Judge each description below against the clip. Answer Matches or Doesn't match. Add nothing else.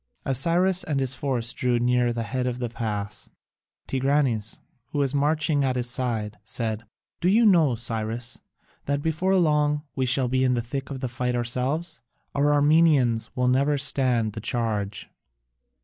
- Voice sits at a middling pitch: Doesn't match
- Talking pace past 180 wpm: Doesn't match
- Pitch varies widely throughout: Doesn't match